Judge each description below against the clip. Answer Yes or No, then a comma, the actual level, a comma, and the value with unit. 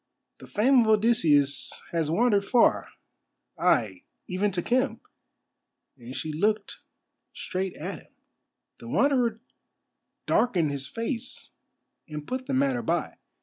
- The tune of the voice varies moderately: No, wide, 7.3 semitones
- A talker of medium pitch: No, high, 210 Hz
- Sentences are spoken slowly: Yes, slow, 115 wpm